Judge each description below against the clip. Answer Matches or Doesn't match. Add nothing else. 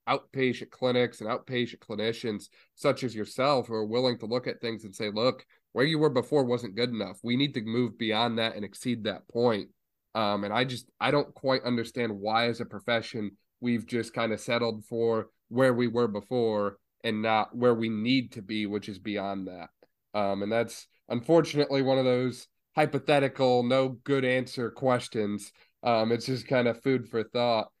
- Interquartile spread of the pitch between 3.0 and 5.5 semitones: Doesn't match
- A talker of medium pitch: Doesn't match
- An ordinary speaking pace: Matches